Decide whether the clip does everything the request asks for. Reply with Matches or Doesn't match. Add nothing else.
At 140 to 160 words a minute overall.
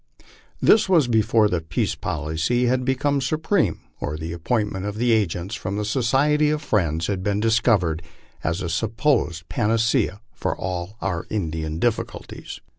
Matches